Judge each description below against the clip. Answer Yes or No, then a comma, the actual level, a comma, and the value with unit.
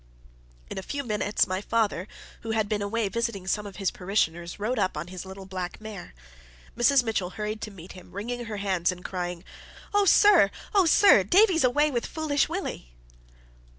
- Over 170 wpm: Yes, average, 185 wpm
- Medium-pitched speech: No, high, 210 Hz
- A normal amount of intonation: Yes, average, 4.5 semitones